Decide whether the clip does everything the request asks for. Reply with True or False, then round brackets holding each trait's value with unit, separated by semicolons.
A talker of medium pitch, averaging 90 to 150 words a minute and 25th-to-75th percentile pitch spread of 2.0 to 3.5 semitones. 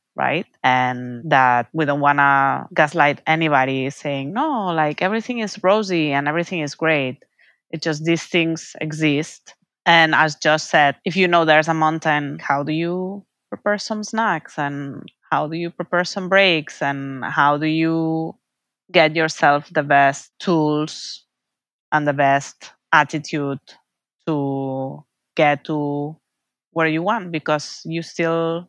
True (155 Hz; 145 wpm; 2.8 semitones)